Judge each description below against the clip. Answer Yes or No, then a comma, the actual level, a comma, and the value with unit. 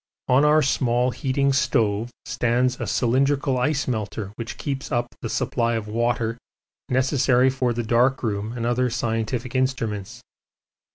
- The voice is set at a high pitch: No, low, 120 Hz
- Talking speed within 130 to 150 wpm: Yes, average, 145 wpm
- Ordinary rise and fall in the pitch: No, narrow, 2.2 semitones